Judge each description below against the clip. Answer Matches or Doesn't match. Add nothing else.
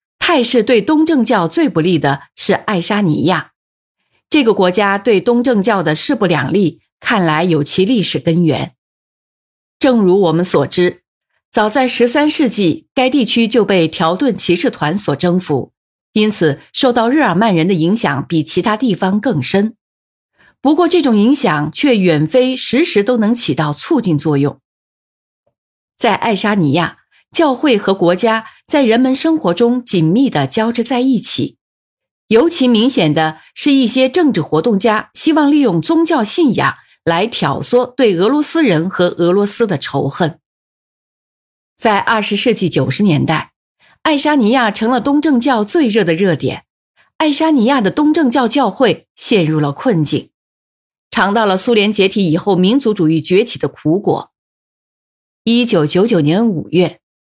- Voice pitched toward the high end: Matches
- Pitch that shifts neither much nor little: Doesn't match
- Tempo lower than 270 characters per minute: Matches